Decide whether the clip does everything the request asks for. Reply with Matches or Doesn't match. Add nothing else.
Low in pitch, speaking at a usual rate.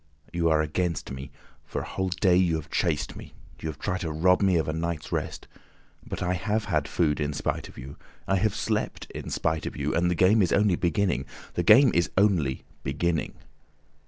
Doesn't match